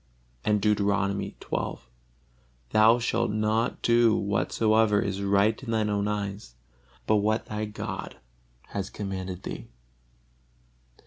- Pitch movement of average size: No, narrow, 1.6 semitones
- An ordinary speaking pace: No, slow, 115 wpm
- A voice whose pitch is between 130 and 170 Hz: No, low, 105 Hz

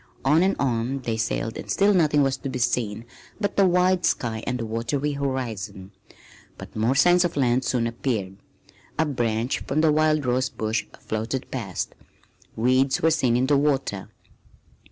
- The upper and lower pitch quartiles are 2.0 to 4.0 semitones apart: No, average, 4.6 semitones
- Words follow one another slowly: No, average, 170 wpm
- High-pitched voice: No, low, 130 Hz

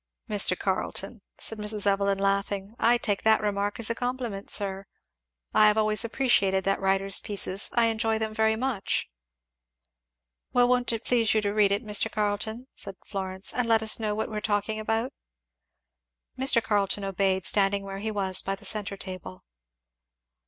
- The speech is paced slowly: No, average, 165 wpm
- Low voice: No, high, 210 Hz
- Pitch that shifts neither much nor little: No, narrow, 2.1 semitones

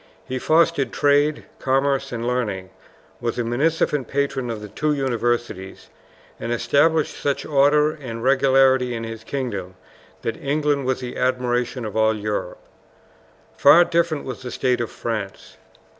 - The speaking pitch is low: Yes, low, 130 Hz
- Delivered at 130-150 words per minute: Yes, average, 145 wpm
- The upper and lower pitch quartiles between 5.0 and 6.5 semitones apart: No, average, 3.5 semitones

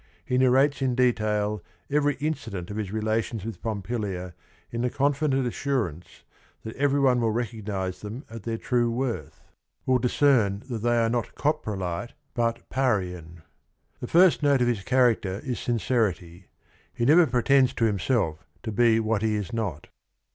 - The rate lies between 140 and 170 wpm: Yes, average, 160 wpm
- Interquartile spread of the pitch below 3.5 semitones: No, average, 3.8 semitones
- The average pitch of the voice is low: Yes, low, 115 Hz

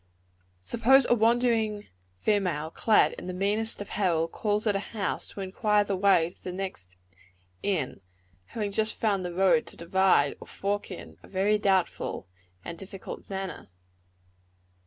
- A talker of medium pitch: No, high, 195 Hz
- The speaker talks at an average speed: Yes, average, 150 wpm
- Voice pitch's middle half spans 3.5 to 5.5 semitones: No, narrow, 2.6 semitones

